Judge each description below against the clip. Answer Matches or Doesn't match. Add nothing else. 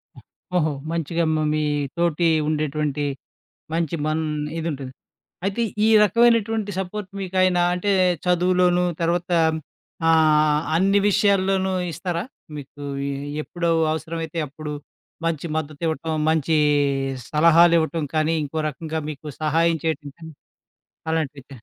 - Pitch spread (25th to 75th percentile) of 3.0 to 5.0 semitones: Doesn't match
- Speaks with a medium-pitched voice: Matches